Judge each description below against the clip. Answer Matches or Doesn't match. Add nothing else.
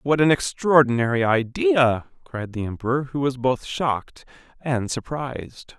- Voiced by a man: Matches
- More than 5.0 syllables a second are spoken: Doesn't match